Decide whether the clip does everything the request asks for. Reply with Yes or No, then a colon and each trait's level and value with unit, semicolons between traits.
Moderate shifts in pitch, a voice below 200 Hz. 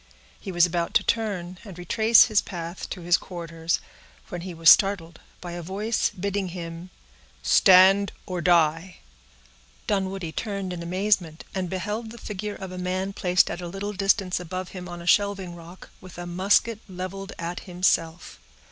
No: narrow, 2.2 semitones; medium, 185 Hz